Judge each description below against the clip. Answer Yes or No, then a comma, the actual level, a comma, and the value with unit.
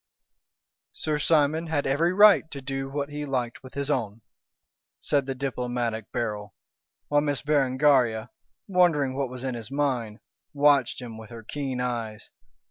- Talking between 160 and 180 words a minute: No, average, 150 wpm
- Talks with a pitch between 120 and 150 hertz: Yes, low, 135 Hz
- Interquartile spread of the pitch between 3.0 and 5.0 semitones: Yes, average, 3.3 semitones